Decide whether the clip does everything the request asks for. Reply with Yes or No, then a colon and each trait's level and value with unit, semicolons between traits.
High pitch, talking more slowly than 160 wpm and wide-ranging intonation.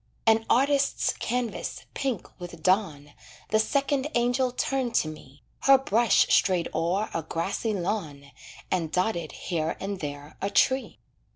Yes: high, 200 Hz; slow, 135 wpm; wide, 6.9 semitones